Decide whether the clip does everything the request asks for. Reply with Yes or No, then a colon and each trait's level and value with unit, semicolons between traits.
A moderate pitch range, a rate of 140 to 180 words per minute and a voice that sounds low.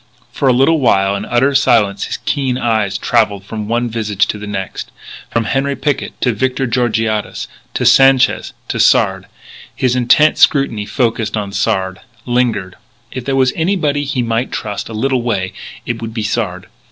Yes: average, 4.0 semitones; average, 170 wpm; low, 115 Hz